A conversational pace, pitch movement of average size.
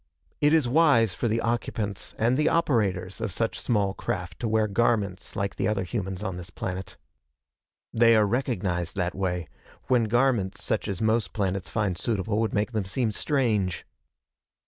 Yes: average, 170 wpm; average, 3.7 semitones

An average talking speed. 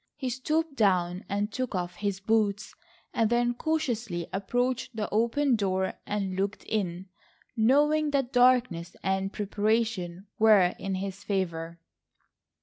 No: slow, 130 wpm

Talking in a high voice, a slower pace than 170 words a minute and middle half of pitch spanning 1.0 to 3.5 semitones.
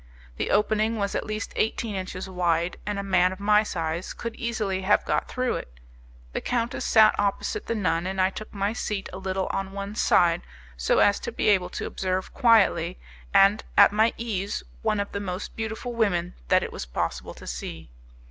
No: high, 200 Hz; average, 195 wpm; average, 2.8 semitones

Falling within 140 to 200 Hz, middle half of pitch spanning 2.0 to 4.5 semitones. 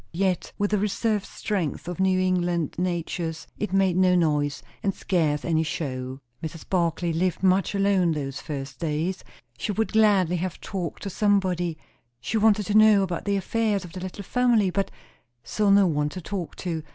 Yes: medium, 185 Hz; average, 3.4 semitones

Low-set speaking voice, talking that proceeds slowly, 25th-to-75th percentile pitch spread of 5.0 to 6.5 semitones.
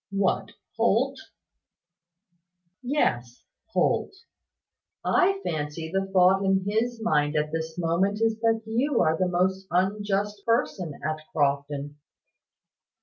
No: high, 190 Hz; slow, 110 wpm; average, 5.3 semitones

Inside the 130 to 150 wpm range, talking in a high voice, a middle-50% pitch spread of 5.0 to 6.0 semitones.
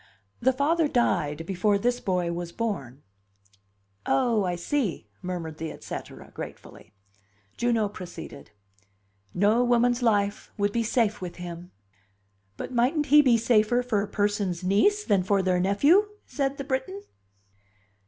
Yes: average, 140 wpm; high, 210 Hz; average, 5.3 semitones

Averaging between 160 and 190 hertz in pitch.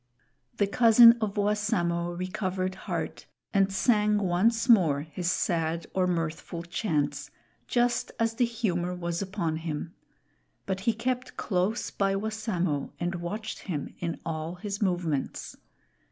Yes: medium, 185 Hz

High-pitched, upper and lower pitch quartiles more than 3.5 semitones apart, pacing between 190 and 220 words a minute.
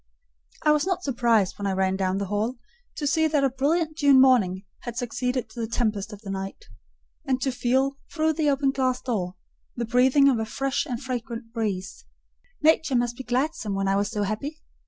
Yes: high, 245 Hz; average, 4.6 semitones; fast, 205 wpm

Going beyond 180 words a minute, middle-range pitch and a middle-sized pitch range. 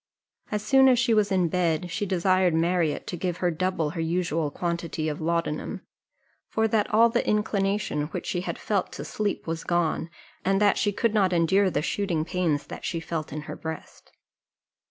Yes: average, 190 wpm; medium, 180 Hz; average, 3.8 semitones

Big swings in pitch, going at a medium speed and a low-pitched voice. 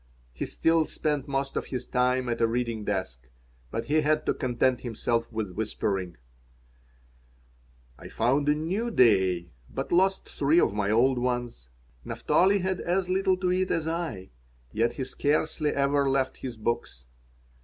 Yes: wide, 5.7 semitones; average, 155 wpm; low, 130 Hz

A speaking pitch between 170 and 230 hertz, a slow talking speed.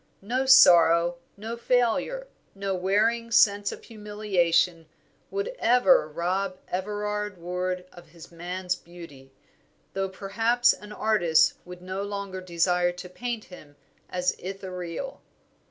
Yes: high, 190 Hz; slow, 120 wpm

